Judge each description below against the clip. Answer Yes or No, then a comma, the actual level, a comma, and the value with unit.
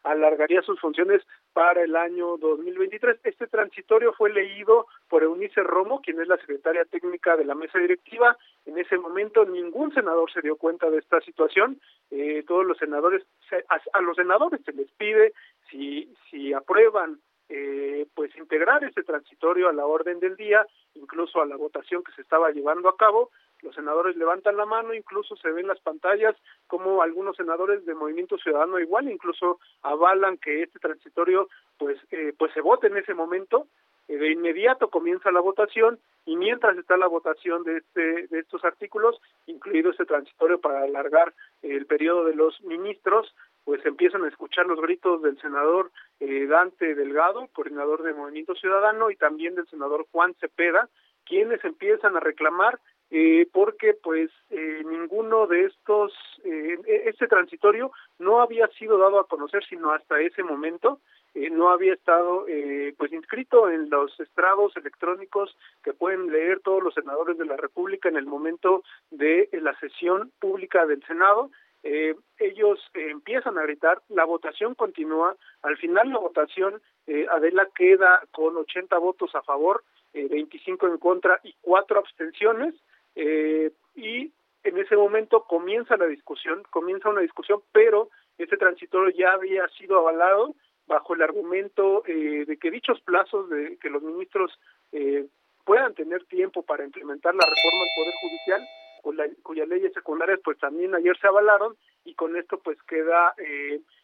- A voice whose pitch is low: No, medium, 185 Hz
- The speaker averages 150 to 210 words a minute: Yes, average, 165 wpm